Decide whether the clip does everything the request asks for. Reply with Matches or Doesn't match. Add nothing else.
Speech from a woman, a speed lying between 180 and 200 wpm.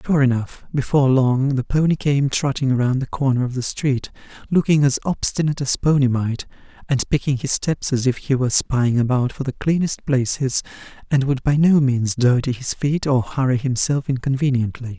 Doesn't match